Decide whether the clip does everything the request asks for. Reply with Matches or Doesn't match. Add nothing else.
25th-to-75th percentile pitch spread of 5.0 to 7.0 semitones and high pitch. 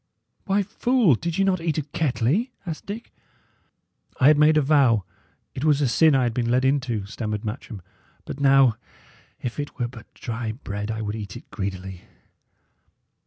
Doesn't match